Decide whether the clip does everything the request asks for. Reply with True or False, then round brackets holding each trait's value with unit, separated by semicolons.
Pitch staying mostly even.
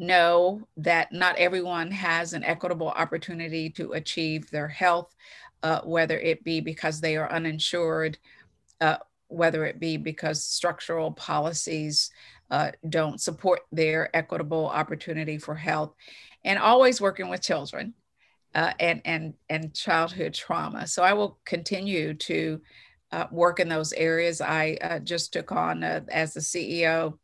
True (1.8 semitones)